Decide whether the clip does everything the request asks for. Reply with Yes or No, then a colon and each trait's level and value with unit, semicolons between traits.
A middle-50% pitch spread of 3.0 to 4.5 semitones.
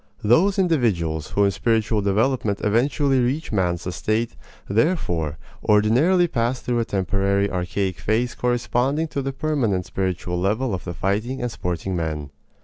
No: wide, 5.4 semitones